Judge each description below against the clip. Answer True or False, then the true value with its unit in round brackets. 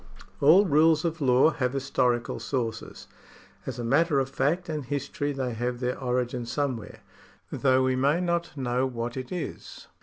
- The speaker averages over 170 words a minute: False (160 wpm)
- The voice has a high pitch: False (135 Hz)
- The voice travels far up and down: False (3.5 semitones)